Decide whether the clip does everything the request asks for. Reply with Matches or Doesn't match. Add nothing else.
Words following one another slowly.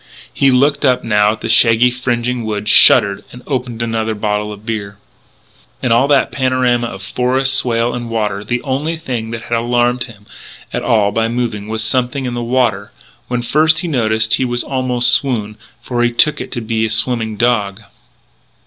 Doesn't match